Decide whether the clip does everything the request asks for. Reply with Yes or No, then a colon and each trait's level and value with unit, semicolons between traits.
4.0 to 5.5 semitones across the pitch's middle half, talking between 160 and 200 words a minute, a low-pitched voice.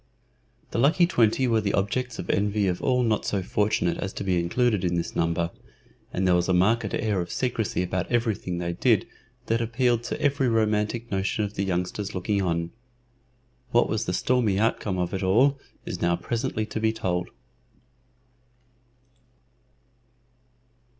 Yes: average, 4.3 semitones; average, 165 wpm; low, 105 Hz